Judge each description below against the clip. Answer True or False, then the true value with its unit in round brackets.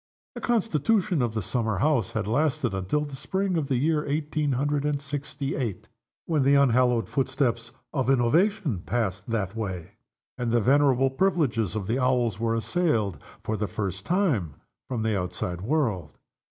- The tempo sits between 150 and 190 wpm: True (165 wpm)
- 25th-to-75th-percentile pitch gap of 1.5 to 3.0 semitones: False (5.2 semitones)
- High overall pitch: False (125 Hz)